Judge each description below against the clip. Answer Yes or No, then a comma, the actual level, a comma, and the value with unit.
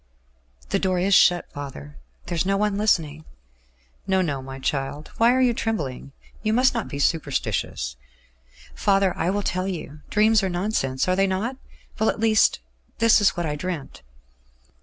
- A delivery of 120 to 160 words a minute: No, average, 170 wpm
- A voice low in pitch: No, medium, 185 Hz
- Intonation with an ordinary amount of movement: No, wide, 6.3 semitones